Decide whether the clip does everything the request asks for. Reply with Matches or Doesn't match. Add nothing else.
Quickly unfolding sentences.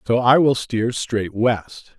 Doesn't match